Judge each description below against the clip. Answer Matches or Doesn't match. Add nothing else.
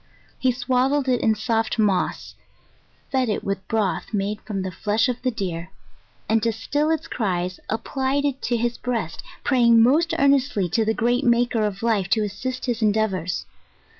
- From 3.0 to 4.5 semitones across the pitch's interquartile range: Matches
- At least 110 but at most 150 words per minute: Doesn't match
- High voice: Matches